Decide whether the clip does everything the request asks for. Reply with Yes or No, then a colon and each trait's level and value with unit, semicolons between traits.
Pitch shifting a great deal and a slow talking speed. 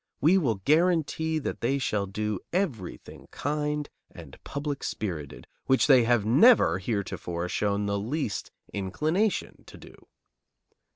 Yes: wide, 7.1 semitones; slow, 125 wpm